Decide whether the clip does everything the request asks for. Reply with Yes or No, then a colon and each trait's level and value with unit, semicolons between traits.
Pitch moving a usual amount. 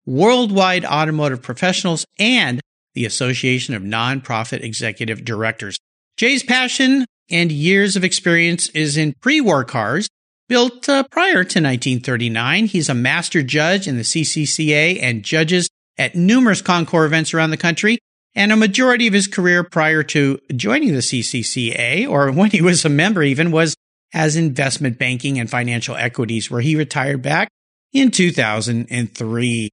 No: wide, 6.7 semitones